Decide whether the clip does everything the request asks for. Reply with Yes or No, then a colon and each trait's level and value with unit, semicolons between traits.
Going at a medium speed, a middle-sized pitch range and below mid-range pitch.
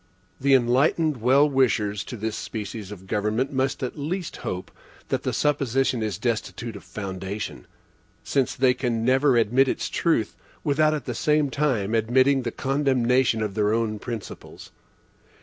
Yes: average, 150 wpm; average, 4.0 semitones; low, 125 Hz